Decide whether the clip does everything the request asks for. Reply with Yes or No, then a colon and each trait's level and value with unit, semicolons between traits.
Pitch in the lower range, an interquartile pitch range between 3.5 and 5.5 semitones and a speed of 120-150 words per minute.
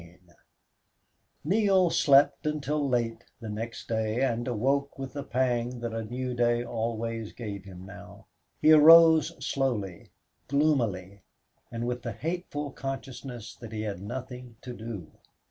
Yes: low, 120 Hz; average, 3.8 semitones; slow, 135 wpm